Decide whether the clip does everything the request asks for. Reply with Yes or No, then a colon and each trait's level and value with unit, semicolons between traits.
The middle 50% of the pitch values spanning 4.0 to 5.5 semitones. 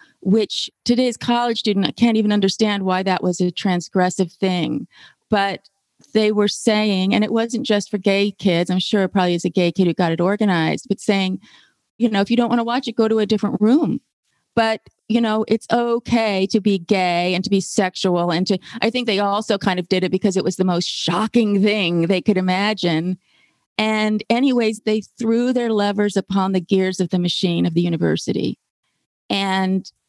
No: average, 2.9 semitones